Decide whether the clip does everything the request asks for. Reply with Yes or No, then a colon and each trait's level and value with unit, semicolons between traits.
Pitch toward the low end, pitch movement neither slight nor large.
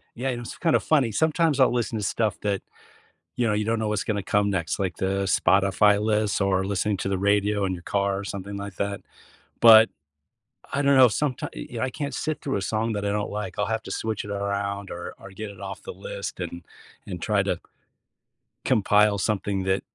No: low, 105 Hz; narrow, 2.2 semitones